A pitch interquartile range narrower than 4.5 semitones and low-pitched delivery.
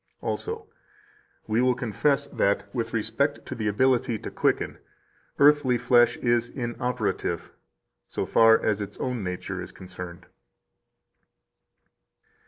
Yes: average, 3.2 semitones; low, 120 Hz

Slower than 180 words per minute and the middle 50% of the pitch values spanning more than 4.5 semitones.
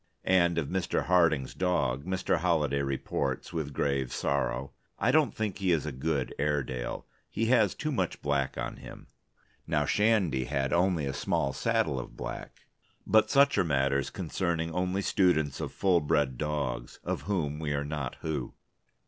Yes: average, 165 wpm; average, 4.9 semitones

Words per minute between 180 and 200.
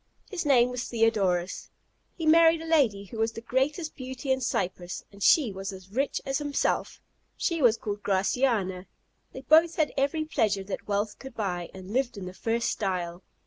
Yes: average, 185 wpm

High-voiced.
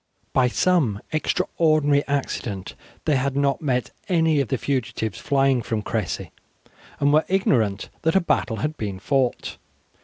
No: medium, 140 Hz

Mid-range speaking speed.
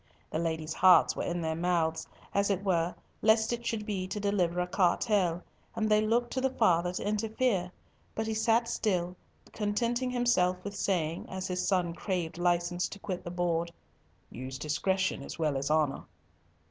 Yes: average, 175 wpm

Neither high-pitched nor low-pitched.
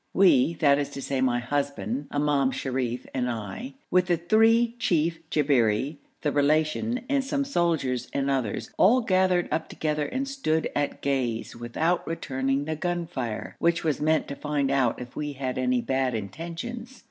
Yes: medium, 150 Hz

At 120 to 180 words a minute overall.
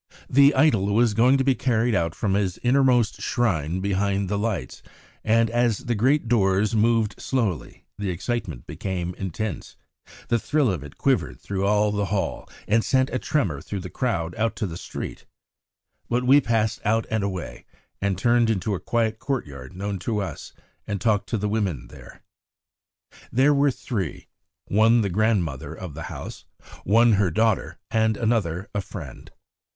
Yes: average, 165 wpm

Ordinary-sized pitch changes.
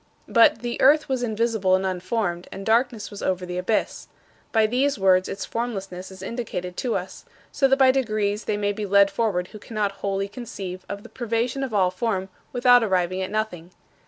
Yes: average, 3.8 semitones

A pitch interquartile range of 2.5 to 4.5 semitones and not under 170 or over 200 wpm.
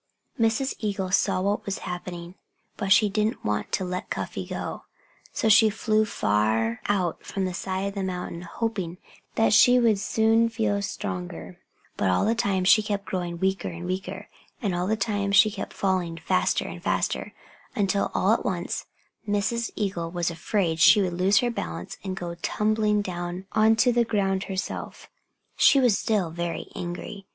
Yes: average, 3.3 semitones; average, 175 wpm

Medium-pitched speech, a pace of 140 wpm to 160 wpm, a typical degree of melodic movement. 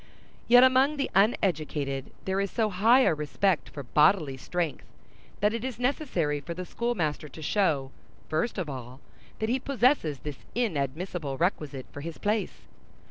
No: medium, 180 Hz; average, 155 wpm; wide, 7.6 semitones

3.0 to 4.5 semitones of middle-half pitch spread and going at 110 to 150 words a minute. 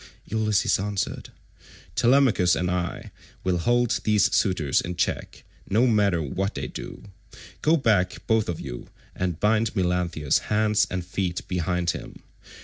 Yes: average, 3.5 semitones; average, 140 wpm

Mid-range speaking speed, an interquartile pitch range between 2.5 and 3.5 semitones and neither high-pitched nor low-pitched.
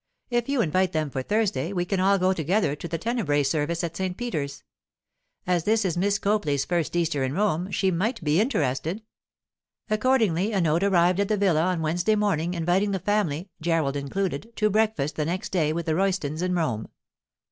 No: average, 185 wpm; average, 4.3 semitones; medium, 180 Hz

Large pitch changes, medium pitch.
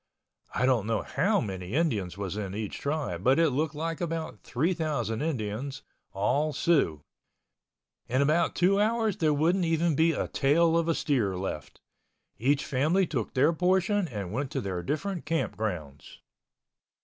Yes: wide, 7.3 semitones; medium, 145 Hz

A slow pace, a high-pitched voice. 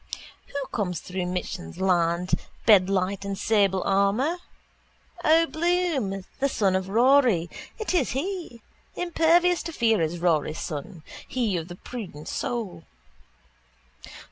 Yes: slow, 115 wpm; high, 200 Hz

